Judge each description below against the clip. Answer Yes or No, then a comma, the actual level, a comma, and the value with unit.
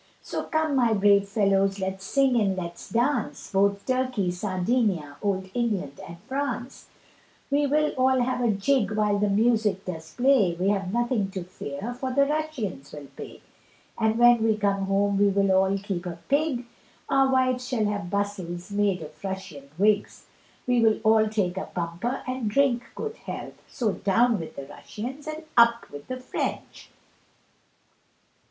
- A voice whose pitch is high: Yes, high, 210 Hz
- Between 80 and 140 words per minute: No, average, 165 wpm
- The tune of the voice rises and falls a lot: No, average, 4.5 semitones